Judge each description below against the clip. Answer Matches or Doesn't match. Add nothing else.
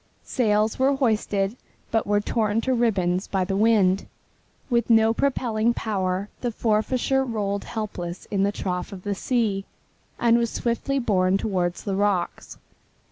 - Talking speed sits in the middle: Matches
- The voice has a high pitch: Matches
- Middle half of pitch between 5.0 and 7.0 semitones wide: Doesn't match